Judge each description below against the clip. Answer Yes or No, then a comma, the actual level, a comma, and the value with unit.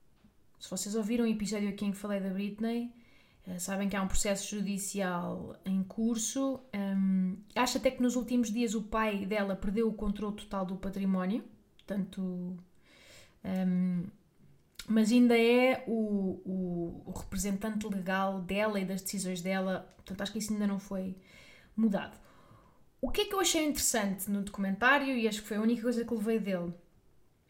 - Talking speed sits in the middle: Yes, average, 170 wpm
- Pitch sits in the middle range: No, high, 200 Hz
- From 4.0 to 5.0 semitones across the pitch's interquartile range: No, average, 2.8 semitones